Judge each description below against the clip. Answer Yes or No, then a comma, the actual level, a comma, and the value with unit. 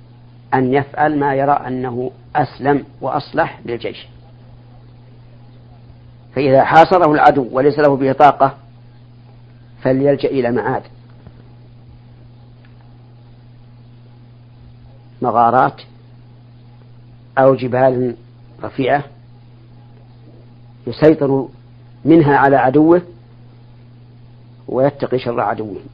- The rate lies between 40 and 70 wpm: Yes, slow, 65 wpm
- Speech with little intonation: Yes, narrow, 1.7 semitones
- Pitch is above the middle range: No, low, 120 Hz